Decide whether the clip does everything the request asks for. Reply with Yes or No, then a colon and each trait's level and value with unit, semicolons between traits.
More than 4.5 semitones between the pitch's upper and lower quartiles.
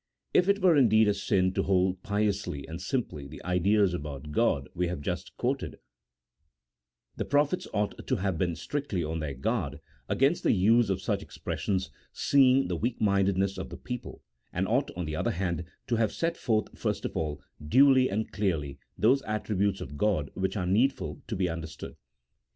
Yes: average, 5.3 semitones